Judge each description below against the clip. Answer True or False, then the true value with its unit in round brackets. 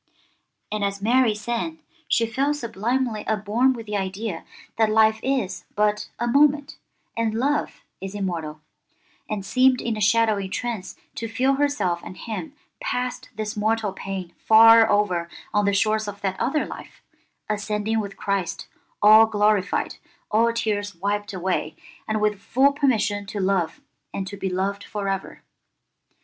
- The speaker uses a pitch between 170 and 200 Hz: False (215 Hz)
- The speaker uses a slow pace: False (150 wpm)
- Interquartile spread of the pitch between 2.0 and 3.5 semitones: True (2.7 semitones)